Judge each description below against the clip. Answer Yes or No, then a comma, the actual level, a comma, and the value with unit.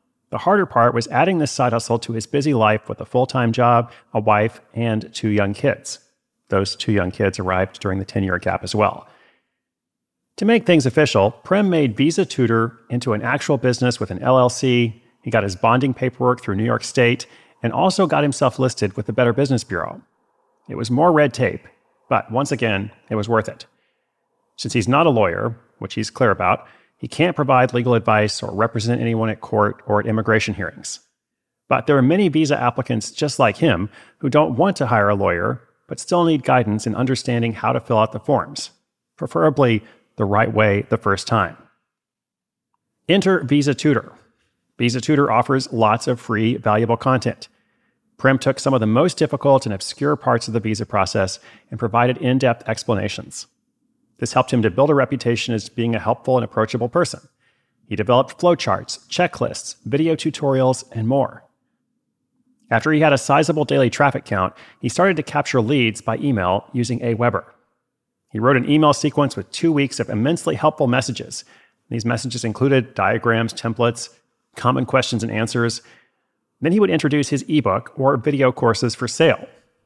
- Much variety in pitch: No, average, 4.0 semitones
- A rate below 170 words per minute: No, average, 180 wpm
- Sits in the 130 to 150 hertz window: No, low, 120 Hz